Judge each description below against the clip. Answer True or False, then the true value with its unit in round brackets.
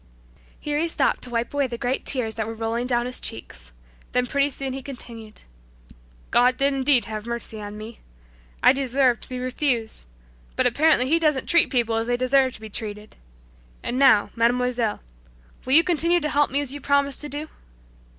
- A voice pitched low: False (250 Hz)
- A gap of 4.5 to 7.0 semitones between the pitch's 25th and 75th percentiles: False (3.4 semitones)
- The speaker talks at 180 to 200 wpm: True (190 wpm)